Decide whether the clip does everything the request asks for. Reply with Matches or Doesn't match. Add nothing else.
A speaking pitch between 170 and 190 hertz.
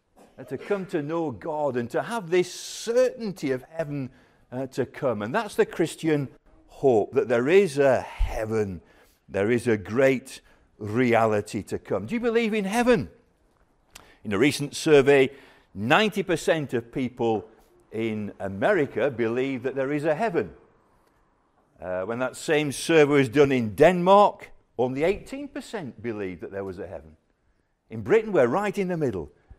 Doesn't match